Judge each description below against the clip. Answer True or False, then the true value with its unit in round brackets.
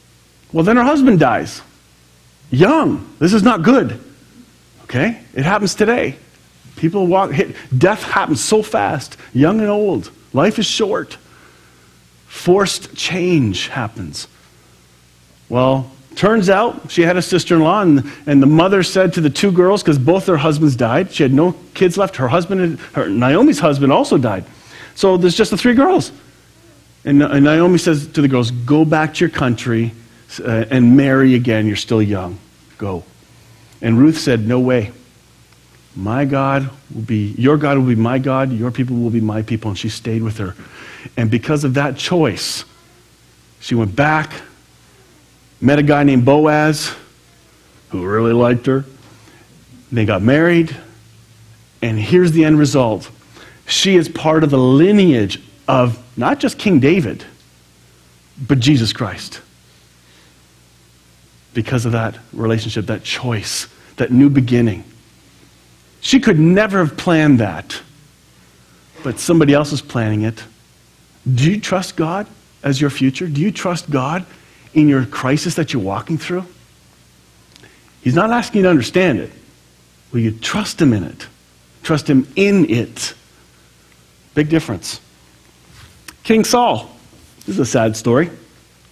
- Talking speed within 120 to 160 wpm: True (150 wpm)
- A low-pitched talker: True (130 Hz)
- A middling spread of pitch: False (7.7 semitones)